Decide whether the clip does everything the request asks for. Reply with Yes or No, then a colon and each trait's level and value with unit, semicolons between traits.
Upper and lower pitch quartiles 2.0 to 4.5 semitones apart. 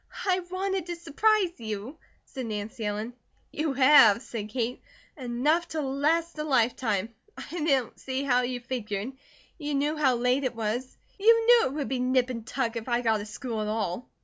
No: average, 4.9 semitones